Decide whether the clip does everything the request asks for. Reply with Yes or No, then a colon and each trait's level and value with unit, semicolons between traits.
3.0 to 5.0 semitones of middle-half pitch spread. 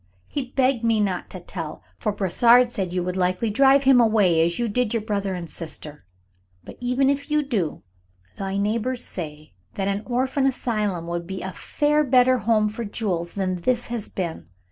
No: wide, 5.4 semitones